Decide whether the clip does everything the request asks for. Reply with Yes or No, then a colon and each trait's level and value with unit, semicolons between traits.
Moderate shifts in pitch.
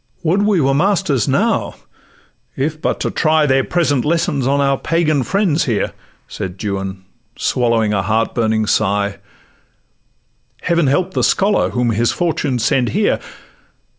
No: wide, 7.0 semitones